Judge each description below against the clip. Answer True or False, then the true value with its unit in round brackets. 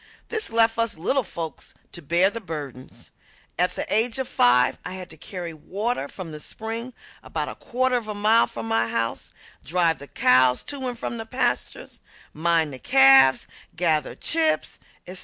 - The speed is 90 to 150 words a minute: False (175 wpm)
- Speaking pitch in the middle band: True (180 Hz)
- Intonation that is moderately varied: False (7.9 semitones)